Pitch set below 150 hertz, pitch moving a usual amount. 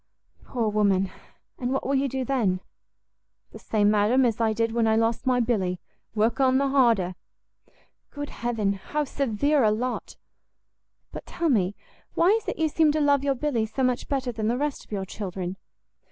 No: high, 235 Hz; average, 4.4 semitones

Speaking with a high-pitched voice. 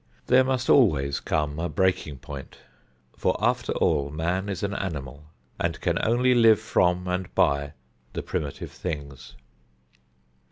No: very low, 85 Hz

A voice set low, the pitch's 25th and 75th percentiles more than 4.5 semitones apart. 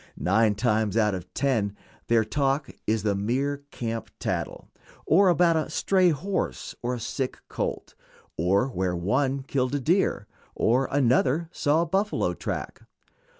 Yes: low, 130 Hz; average, 5.2 semitones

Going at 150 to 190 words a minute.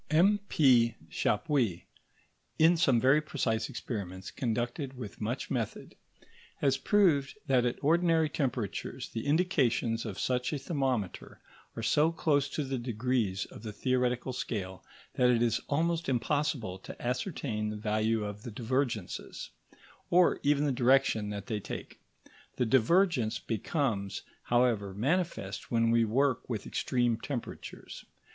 No: slow, 135 wpm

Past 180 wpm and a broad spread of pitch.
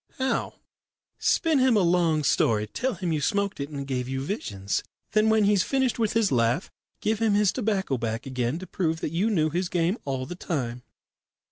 Yes: fast, 205 wpm; wide, 7.8 semitones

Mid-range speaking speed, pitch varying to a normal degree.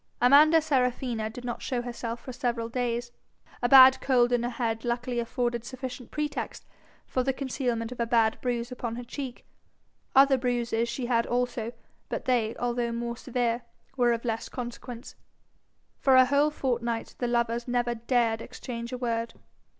No: average, 165 wpm; narrow, 1.3 semitones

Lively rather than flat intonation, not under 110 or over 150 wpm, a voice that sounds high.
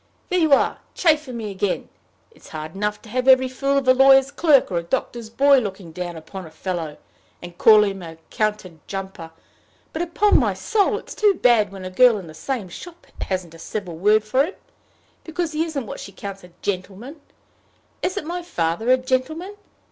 No: wide, 7.0 semitones; average, 195 wpm; high, 220 Hz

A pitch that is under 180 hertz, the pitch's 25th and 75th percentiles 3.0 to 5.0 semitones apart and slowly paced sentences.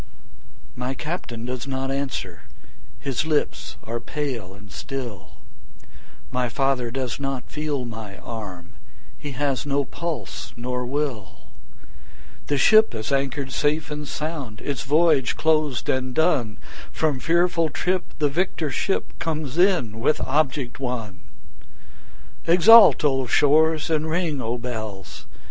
Yes: low, 135 Hz; average, 4.2 semitones; slow, 130 wpm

